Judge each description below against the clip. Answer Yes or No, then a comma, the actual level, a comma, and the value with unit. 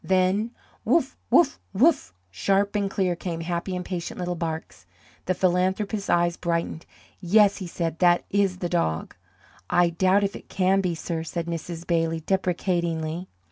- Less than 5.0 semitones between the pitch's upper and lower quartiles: Yes, narrow, 2.5 semitones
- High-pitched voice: No, medium, 180 Hz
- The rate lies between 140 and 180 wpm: Yes, average, 150 wpm